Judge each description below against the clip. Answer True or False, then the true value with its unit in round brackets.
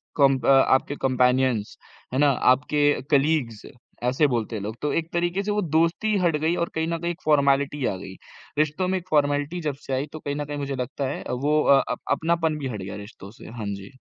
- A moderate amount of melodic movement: True (3.7 semitones)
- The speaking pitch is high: False (145 Hz)